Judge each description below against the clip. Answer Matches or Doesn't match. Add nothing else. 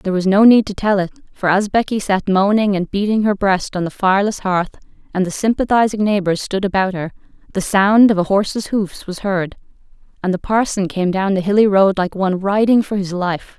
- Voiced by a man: Doesn't match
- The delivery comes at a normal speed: Doesn't match